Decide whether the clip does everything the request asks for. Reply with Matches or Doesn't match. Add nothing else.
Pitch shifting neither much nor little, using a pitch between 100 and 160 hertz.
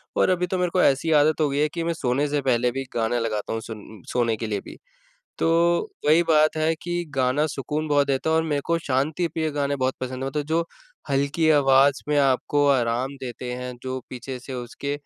Matches